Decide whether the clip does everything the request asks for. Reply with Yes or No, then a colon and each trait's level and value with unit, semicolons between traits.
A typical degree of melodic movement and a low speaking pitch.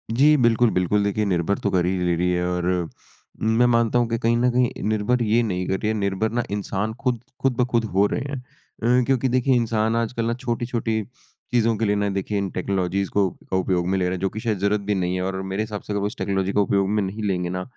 Yes: average, 3.4 semitones; low, 105 Hz